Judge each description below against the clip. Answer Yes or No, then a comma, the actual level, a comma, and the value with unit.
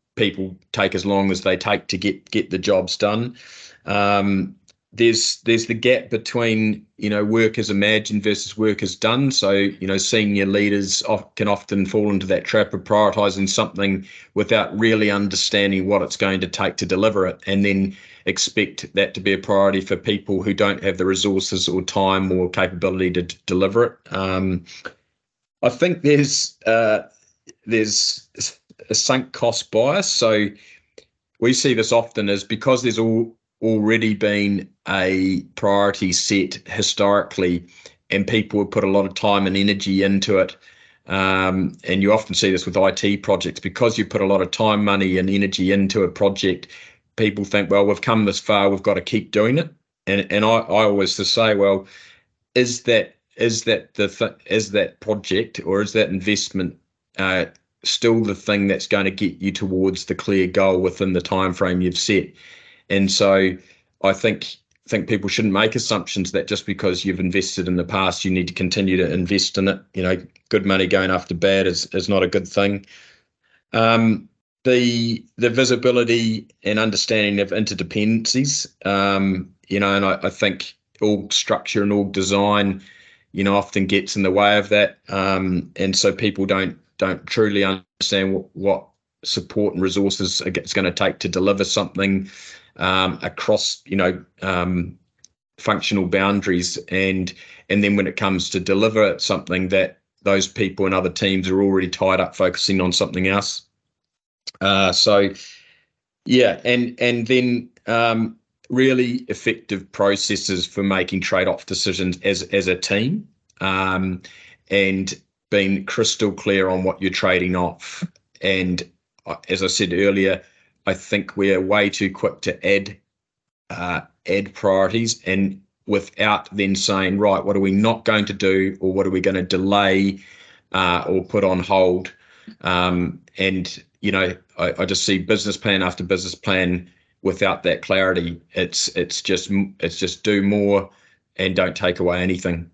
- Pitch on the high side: No, low, 100 Hz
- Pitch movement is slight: Yes, narrow, 1.9 semitones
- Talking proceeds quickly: No, average, 170 wpm